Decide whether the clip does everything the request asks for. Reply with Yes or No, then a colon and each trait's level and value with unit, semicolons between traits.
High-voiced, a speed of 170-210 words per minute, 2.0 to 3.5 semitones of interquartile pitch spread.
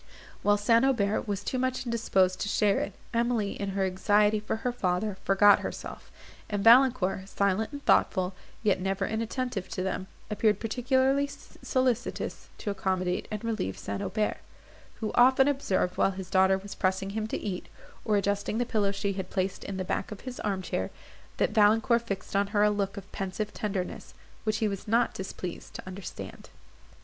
Yes: high, 205 Hz; average, 180 wpm; average, 3.0 semitones